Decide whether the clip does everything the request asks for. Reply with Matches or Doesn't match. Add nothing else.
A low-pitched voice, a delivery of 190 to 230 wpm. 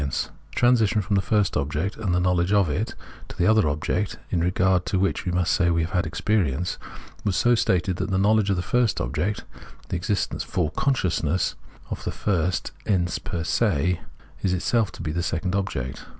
Matches